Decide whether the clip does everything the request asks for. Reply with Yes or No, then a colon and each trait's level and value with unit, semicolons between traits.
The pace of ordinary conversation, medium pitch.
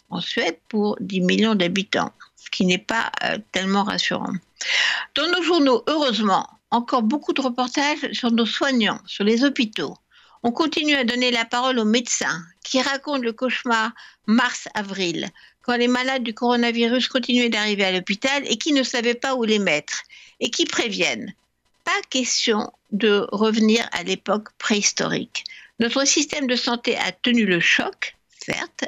No: average, 160 wpm; high, 240 Hz